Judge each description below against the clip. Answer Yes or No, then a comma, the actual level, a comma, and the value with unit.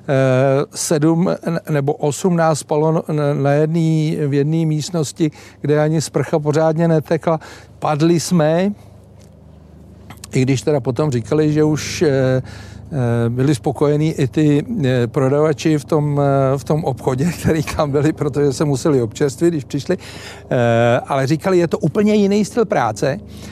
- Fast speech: No, average, 130 wpm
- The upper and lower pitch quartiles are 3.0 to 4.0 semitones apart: Yes, average, 3.4 semitones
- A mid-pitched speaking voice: Yes, medium, 150 Hz